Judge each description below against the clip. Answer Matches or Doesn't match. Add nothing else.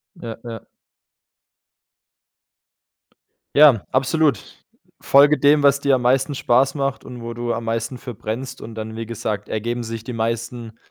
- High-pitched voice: Doesn't match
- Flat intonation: Doesn't match